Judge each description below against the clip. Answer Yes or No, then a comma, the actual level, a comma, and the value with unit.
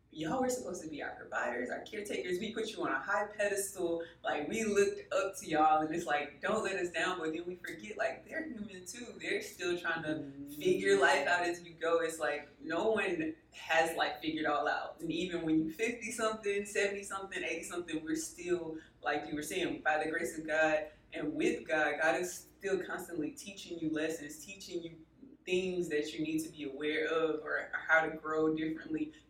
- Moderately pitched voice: Yes, medium, 165 Hz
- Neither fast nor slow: No, fast, 210 wpm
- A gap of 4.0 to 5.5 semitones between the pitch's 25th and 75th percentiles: Yes, average, 4.4 semitones